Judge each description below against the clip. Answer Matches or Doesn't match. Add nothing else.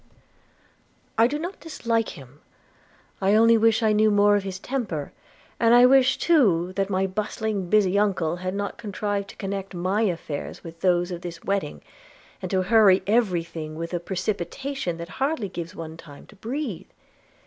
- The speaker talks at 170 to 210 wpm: Matches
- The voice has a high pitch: Matches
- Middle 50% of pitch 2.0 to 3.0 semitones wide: Doesn't match